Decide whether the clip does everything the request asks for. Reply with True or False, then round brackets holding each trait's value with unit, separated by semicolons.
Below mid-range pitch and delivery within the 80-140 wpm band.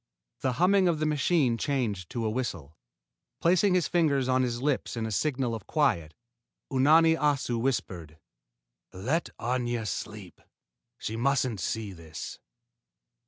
True (130 Hz; 135 wpm)